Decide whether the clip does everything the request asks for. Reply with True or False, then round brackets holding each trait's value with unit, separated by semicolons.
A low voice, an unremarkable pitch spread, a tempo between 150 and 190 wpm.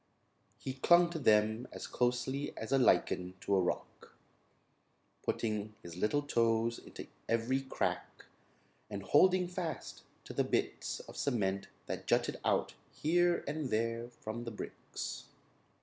False (120 Hz; 5.0 semitones; 135 wpm)